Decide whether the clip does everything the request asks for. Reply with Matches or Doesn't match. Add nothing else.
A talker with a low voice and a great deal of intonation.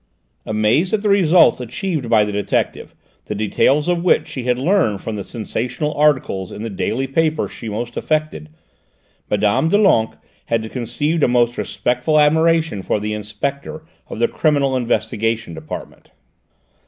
Matches